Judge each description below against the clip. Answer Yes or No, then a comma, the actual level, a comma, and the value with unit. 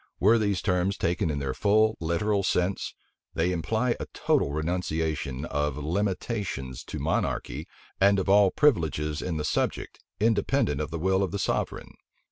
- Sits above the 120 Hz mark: No, very low, 90 Hz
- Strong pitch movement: No, average, 4.7 semitones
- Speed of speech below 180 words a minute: Yes, average, 155 wpm